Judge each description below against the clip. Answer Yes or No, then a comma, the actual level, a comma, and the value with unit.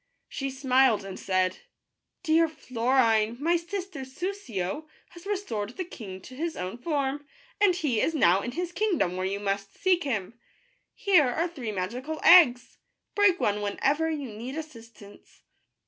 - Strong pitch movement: Yes, wide, 7.8 semitones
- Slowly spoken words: No, average, 160 wpm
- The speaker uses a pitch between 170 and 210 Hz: No, very high, 265 Hz